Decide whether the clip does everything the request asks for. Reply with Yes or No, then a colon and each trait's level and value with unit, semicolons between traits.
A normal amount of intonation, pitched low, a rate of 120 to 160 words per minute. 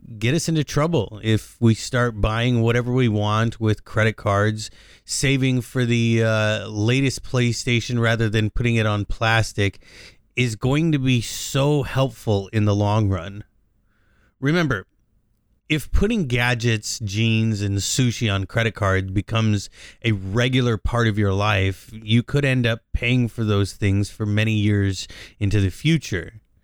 Yes: average, 3.0 semitones; low, 110 Hz; average, 150 wpm